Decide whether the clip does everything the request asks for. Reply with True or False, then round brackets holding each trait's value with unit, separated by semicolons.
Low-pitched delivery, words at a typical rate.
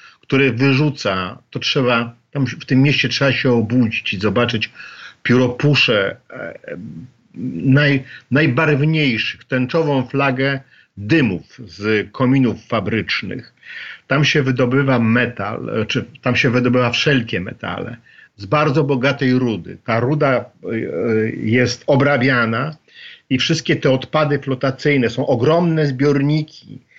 False (130 Hz; 105 wpm)